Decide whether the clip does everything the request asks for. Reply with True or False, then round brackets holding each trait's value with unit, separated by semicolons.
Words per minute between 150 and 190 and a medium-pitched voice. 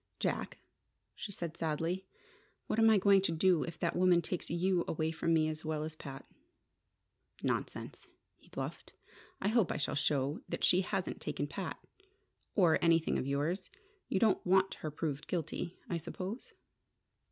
True (165 wpm; 170 Hz)